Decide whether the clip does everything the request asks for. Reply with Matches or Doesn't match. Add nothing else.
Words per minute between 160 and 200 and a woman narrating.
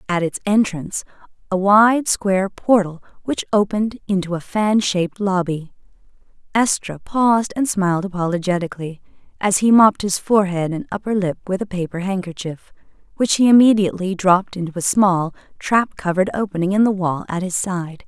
Doesn't match